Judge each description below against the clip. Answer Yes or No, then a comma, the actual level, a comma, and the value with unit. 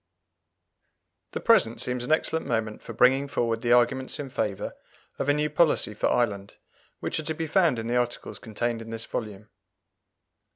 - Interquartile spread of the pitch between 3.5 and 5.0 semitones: Yes, average, 4.2 semitones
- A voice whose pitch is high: No, low, 120 Hz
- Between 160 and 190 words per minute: Yes, average, 175 wpm